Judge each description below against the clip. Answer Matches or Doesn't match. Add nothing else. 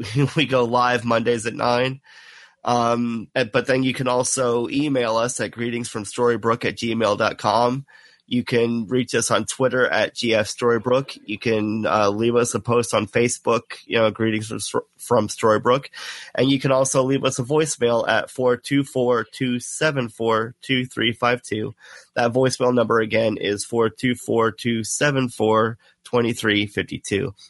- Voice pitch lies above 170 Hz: Doesn't match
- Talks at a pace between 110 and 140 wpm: Matches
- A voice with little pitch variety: Matches